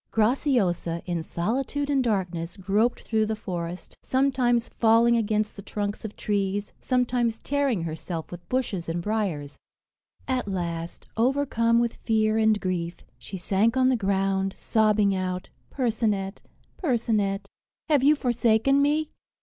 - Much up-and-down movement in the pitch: No, average, 4.2 semitones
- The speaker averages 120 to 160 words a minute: Yes, slow, 135 wpm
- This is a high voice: Yes, high, 215 Hz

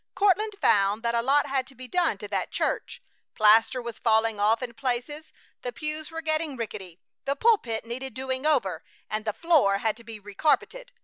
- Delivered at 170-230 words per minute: Yes, average, 190 wpm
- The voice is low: No, very high, 250 Hz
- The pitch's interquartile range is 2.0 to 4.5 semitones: No, wide, 5.6 semitones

